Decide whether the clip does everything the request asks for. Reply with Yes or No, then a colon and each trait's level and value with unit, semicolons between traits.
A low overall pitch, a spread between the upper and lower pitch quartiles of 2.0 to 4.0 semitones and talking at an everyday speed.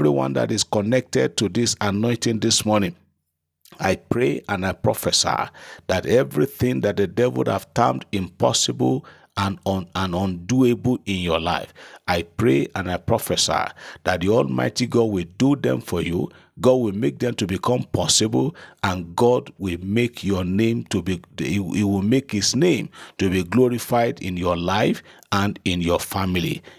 No: low, 100 Hz; average, 4.8 semitones; average, 170 wpm